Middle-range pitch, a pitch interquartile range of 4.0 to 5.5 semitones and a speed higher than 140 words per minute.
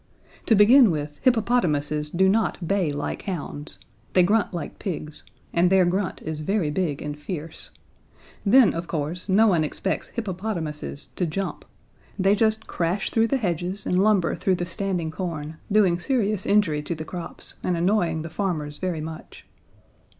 Yes: medium, 180 Hz; average, 4.3 semitones; average, 160 wpm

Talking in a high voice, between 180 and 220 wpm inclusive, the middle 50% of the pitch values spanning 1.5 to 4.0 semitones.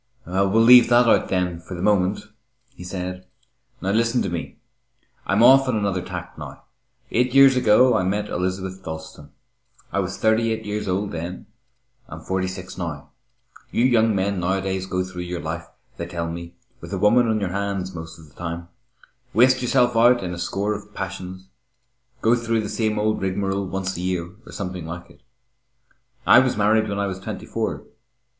No: very low, 95 Hz; average, 190 wpm; average, 3.4 semitones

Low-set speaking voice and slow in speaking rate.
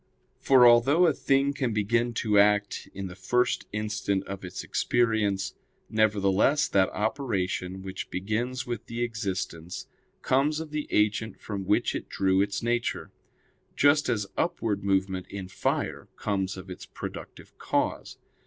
No: low, 105 Hz; average, 145 wpm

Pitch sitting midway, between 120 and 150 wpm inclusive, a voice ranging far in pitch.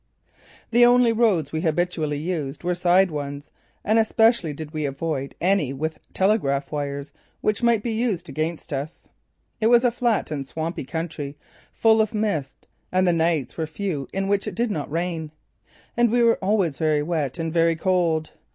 No: medium, 170 Hz; average, 175 wpm; wide, 5.7 semitones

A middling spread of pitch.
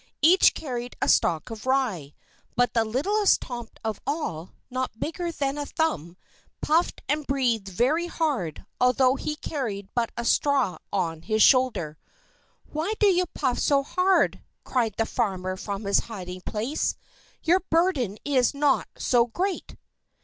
No: wide, 6.2 semitones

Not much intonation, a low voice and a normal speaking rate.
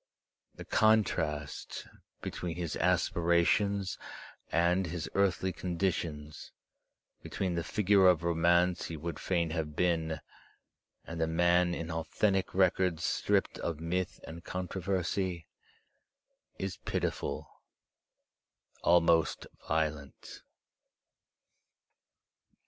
No: narrow, 2.2 semitones; very low, 85 Hz; slow, 90 wpm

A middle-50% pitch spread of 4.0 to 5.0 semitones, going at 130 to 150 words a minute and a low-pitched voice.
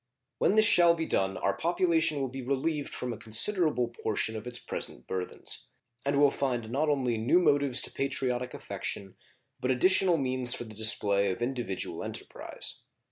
No: average, 4.6 semitones; average, 170 wpm; low, 130 Hz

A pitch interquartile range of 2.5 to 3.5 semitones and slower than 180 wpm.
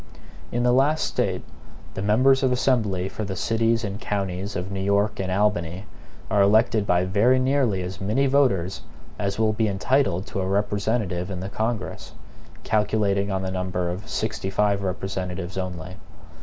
Yes: average, 2.9 semitones; average, 165 wpm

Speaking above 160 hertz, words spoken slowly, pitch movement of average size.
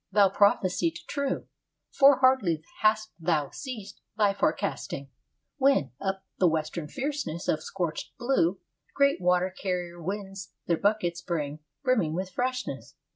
No: high, 190 Hz; slow, 130 wpm; wide, 5.9 semitones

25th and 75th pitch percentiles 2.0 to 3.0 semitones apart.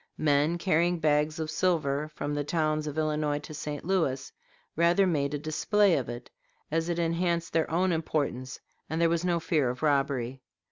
Yes: narrow, 2.6 semitones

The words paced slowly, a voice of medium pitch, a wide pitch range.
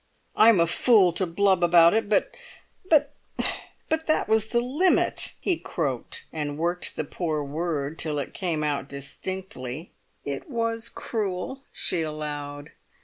Yes: slow, 125 wpm; medium, 175 Hz; wide, 6.8 semitones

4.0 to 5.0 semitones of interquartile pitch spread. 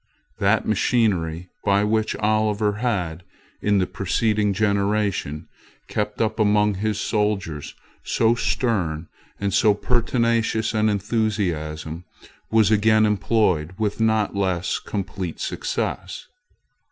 No: narrow, 2.6 semitones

